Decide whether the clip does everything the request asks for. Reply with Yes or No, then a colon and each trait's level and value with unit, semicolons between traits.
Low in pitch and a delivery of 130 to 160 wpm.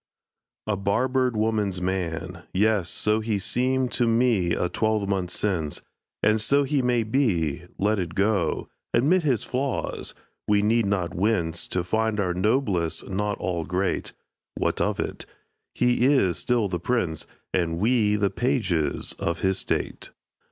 Yes: low, 105 Hz; average, 145 wpm